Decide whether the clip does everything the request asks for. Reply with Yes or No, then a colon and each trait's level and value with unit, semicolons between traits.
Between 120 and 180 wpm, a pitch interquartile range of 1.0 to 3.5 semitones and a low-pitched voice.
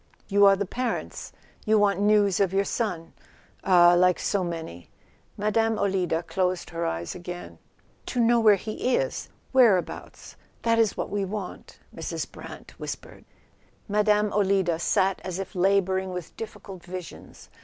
No: average, 145 wpm; average, 2.8 semitones; high, 195 Hz